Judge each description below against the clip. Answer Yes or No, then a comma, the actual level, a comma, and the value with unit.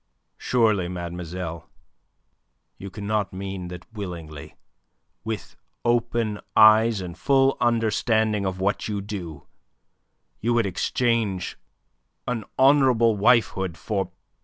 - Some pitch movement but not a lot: Yes, average, 3.9 semitones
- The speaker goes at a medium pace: No, slow, 105 wpm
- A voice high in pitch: No, low, 105 Hz